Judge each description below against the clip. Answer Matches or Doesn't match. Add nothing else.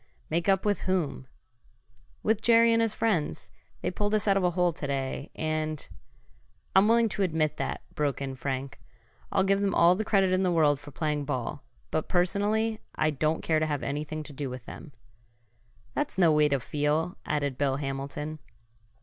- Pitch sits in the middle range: Matches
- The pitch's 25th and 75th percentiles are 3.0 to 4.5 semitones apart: Doesn't match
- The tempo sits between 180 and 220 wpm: Matches